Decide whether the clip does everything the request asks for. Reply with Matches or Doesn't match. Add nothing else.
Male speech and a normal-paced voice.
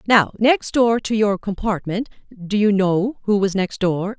Doesn't match